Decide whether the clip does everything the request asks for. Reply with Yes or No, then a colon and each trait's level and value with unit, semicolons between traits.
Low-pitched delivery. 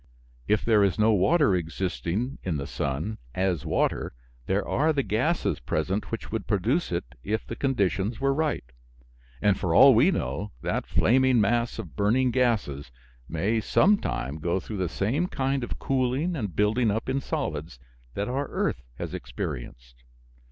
Yes: low, 110 Hz